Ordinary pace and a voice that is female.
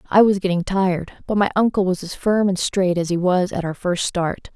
No: fast, 250 wpm; female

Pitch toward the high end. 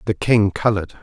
No: low, 100 Hz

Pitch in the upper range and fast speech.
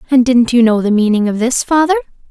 Yes: high, 240 Hz; fast, 235 wpm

